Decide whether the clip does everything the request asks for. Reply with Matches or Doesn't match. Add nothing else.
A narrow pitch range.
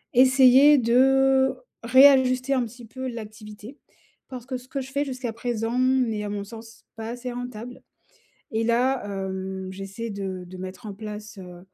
Doesn't match